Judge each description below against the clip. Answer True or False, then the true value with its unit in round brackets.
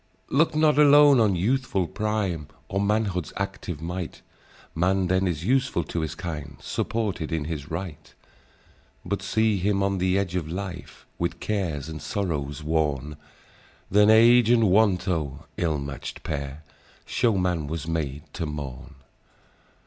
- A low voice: True (90 Hz)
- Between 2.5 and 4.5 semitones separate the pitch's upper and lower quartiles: False (4.9 semitones)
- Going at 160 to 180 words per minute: False (140 wpm)